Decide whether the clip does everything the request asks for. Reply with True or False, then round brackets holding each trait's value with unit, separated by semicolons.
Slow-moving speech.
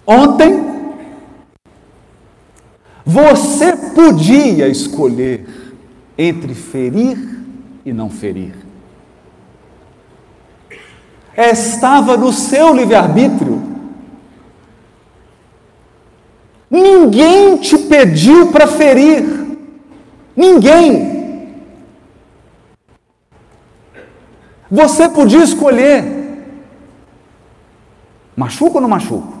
True (55 wpm)